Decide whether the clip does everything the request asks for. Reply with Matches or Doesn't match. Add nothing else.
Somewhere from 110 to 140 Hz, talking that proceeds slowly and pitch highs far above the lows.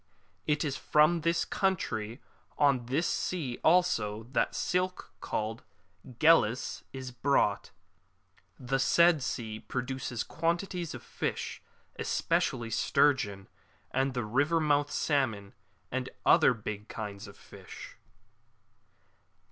Matches